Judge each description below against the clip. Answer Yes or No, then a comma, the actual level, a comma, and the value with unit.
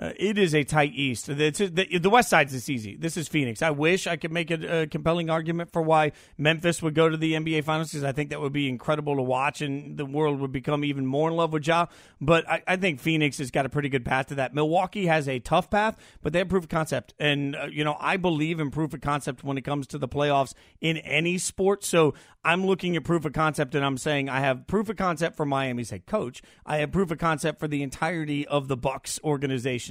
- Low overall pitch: No, medium, 155 Hz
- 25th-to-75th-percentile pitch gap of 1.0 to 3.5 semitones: Yes, average, 3.0 semitones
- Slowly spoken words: No, fast, 255 wpm